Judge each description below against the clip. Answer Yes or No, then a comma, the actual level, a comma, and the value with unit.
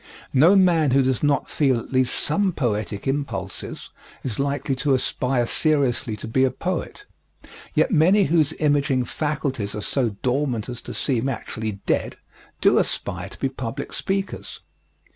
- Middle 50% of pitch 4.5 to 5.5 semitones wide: No, average, 3.7 semitones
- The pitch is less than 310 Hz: Yes, low, 135 Hz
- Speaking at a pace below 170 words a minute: Yes, average, 155 wpm